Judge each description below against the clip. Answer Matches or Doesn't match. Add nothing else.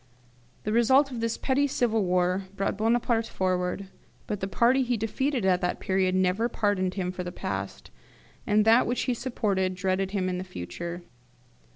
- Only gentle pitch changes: Doesn't match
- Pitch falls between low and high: Doesn't match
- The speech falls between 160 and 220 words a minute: Matches